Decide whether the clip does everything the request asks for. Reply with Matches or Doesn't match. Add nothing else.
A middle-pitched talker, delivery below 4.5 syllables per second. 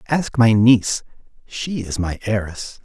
Doesn't match